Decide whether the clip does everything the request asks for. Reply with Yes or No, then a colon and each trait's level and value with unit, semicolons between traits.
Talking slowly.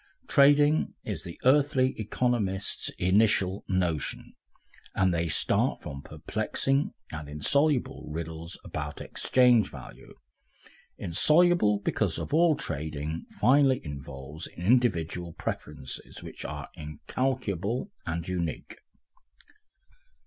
Yes: slow, 90 wpm